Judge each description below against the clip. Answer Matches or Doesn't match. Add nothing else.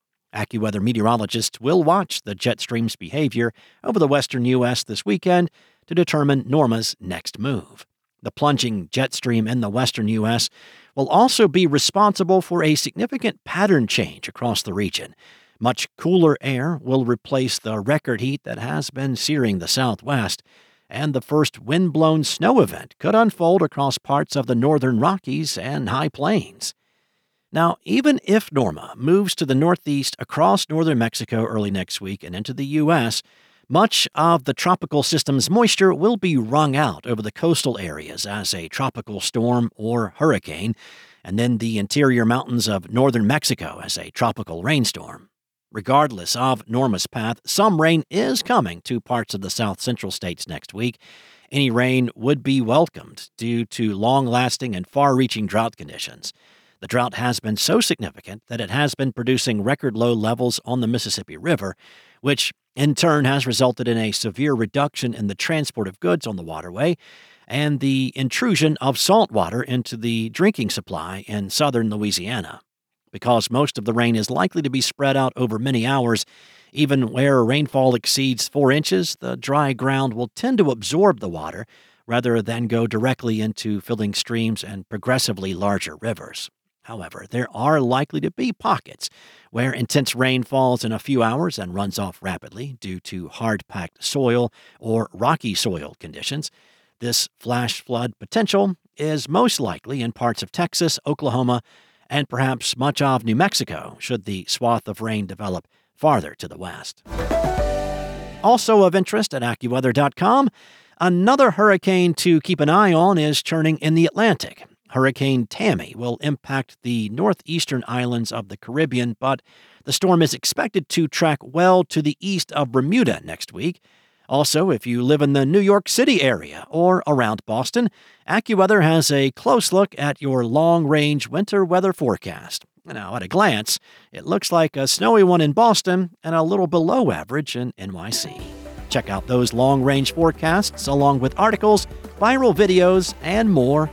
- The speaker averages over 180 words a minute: Doesn't match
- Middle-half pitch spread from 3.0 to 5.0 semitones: Doesn't match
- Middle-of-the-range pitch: Doesn't match